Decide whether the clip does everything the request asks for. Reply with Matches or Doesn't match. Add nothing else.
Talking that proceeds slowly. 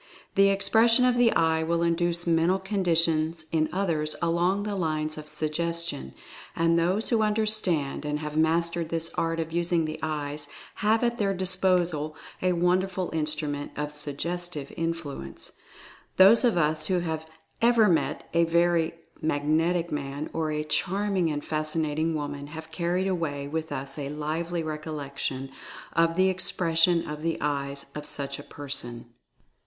Doesn't match